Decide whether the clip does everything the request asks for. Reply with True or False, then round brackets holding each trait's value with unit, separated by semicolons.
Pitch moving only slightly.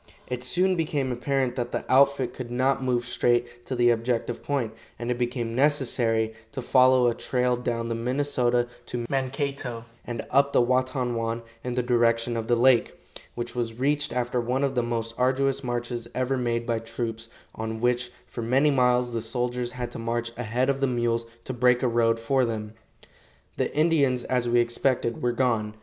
True (1.7 semitones)